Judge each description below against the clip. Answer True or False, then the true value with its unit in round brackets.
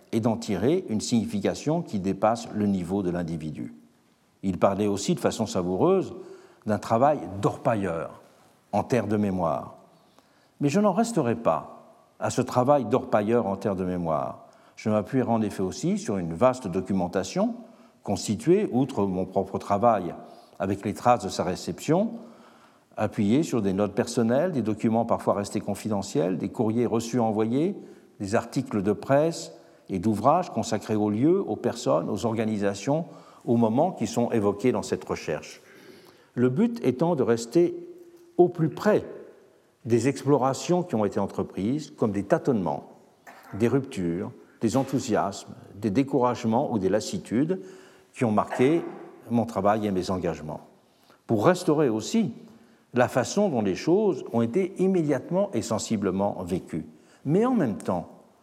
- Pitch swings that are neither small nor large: False (6.6 semitones)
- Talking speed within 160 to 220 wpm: False (150 wpm)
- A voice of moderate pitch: False (115 Hz)